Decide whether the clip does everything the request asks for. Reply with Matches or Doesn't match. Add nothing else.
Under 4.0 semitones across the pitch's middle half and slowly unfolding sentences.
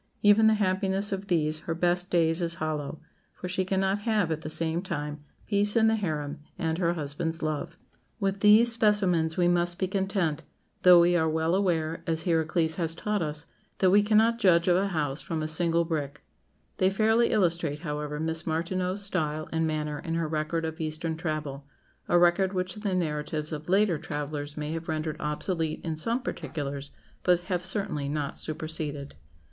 Doesn't match